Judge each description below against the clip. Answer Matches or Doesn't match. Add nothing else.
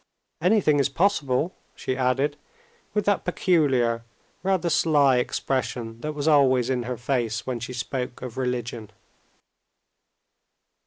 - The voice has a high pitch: Doesn't match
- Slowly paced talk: Matches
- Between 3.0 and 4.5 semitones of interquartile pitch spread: Matches